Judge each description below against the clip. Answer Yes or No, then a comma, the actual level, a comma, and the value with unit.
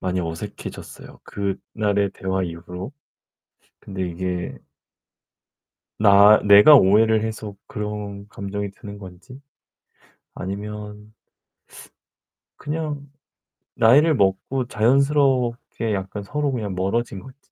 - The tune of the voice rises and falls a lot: No, average, 3.6 semitones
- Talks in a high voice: No, low, 105 Hz